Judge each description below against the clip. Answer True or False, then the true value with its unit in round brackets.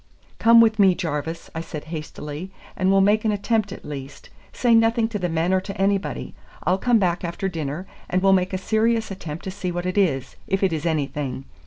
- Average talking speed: False (215 wpm)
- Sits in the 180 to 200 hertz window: True (185 Hz)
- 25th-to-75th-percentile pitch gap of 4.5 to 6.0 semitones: False (4.0 semitones)